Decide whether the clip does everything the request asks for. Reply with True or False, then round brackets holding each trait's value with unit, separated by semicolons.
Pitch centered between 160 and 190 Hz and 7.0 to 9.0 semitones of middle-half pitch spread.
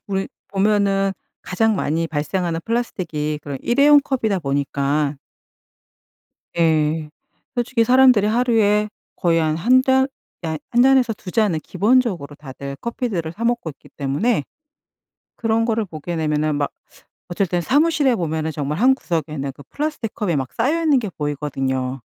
True (185 Hz; 7.6 semitones)